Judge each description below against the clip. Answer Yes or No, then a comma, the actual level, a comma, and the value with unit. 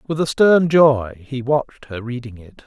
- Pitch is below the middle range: Yes, low, 130 Hz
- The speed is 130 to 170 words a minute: No, fast, 205 wpm